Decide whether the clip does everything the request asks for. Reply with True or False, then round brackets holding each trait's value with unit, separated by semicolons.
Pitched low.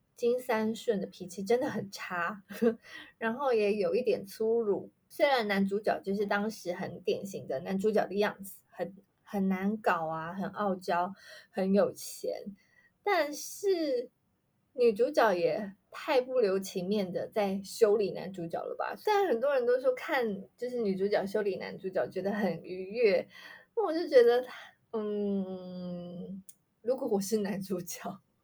False (210 Hz)